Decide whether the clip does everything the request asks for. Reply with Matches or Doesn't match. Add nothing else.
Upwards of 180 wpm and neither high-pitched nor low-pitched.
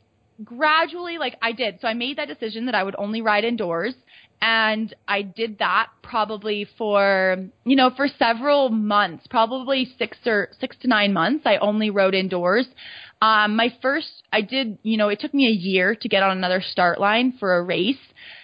Doesn't match